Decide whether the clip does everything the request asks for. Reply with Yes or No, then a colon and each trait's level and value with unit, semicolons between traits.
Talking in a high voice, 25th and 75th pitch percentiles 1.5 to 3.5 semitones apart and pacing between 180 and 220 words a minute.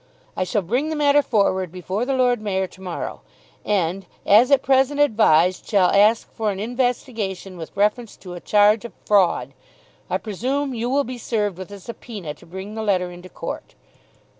No: high, 210 Hz; average, 4.7 semitones; average, 185 wpm